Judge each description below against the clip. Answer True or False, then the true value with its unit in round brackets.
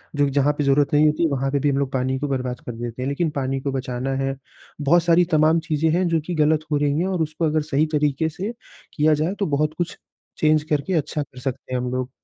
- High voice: False (145 Hz)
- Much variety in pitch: False (2.7 semitones)